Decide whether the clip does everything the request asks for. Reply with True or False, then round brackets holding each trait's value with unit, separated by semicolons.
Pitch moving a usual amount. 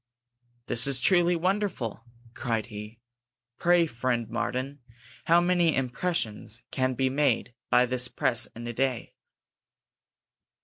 False (5.9 semitones)